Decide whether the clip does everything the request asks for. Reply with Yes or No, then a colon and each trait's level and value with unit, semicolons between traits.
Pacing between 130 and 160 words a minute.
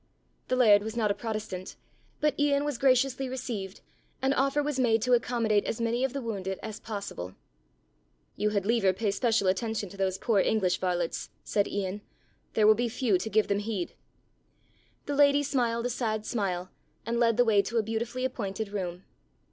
No: average, 185 wpm